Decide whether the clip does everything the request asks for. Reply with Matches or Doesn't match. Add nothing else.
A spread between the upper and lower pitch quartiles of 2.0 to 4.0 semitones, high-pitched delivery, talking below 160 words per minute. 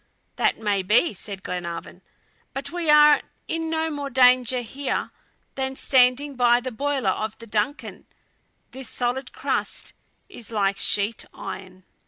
Doesn't match